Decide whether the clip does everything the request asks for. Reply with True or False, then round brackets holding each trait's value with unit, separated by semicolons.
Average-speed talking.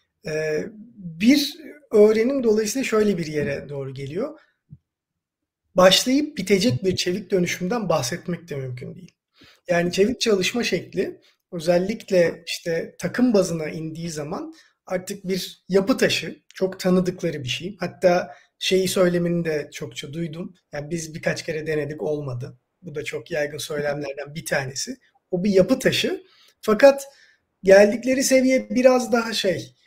True (130 wpm)